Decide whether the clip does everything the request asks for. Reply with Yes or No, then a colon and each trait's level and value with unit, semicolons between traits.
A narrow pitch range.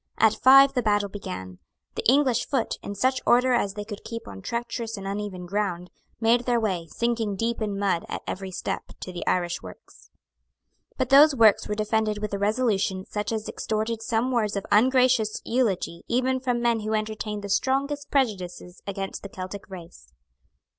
No: average, 3.4 semitones